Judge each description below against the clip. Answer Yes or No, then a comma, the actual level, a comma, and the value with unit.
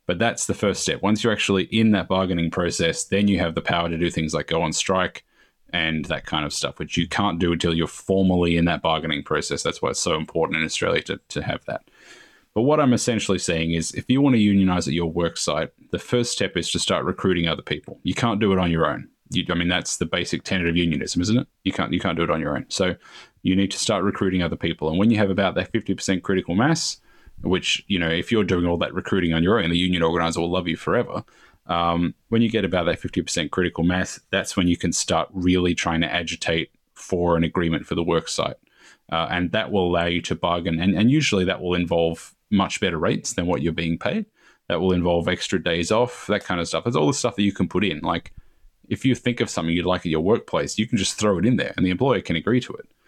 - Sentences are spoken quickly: Yes, fast, 260 wpm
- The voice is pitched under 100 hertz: Yes, very low, 90 Hz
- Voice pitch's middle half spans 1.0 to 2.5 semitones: No, average, 2.9 semitones